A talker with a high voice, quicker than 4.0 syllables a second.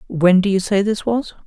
Yes: high, 200 Hz; 5.0 syllables/s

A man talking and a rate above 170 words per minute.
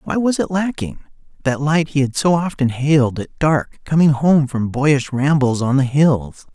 Yes: male; average, 195 wpm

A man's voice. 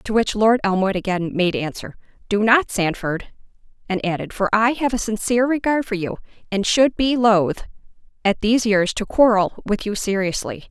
No: female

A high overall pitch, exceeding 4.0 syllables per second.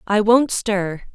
No: high, 210 Hz; 3.3 syllables/s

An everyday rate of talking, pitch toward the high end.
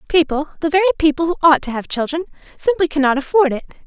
Yes: average, 170 wpm; very high, 310 Hz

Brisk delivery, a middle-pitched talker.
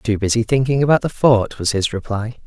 No: fast, 220 wpm; low, 115 Hz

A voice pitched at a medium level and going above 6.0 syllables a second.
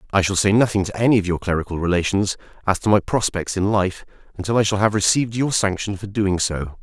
No: low, 100 Hz; 6.2 syllables/s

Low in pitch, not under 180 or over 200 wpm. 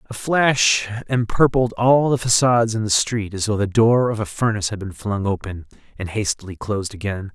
Yes: low, 110 Hz; average, 195 wpm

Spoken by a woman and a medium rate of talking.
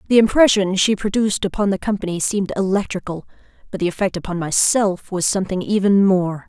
Yes: female; average, 165 wpm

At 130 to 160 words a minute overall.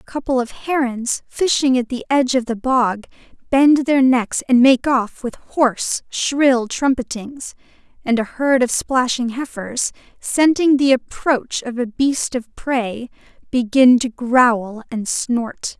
Yes: average, 150 wpm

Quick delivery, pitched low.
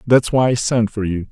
Yes: fast, 275 wpm; low, 115 Hz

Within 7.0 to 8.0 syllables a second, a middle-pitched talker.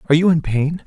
Yes: 7.5 syllables/s; medium, 155 Hz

